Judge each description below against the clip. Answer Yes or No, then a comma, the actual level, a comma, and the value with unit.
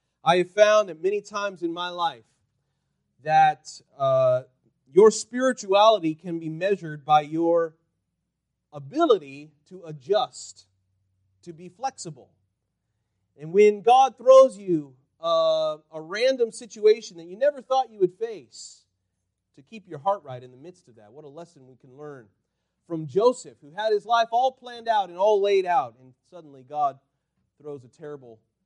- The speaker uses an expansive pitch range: Yes, wide, 7.5 semitones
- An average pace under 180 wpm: Yes, average, 155 wpm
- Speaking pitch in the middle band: Yes, medium, 165 Hz